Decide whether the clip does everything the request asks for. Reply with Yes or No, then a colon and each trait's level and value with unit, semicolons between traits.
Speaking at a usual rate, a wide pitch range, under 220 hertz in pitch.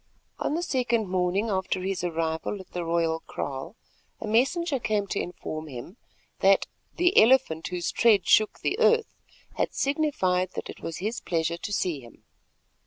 Yes: average, 165 wpm; wide, 6.0 semitones; high, 190 Hz